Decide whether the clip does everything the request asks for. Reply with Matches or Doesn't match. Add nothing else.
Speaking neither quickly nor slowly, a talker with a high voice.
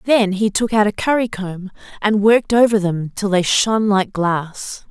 Matches